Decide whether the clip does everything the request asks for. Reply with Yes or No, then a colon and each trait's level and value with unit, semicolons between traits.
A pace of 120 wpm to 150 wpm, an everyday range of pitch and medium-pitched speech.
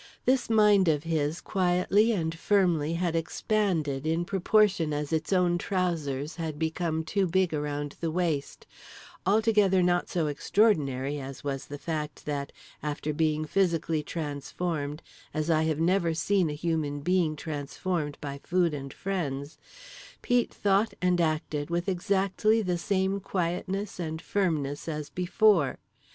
Yes: average, 140 wpm; average, 3.9 semitones; medium, 165 Hz